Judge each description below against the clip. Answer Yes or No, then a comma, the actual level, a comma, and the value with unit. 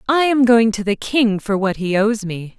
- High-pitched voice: Yes, high, 220 Hz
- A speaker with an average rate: No, fast, 255 wpm